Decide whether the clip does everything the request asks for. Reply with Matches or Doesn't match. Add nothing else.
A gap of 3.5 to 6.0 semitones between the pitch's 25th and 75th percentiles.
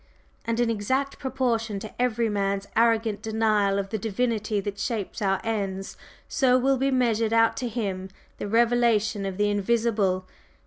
Doesn't match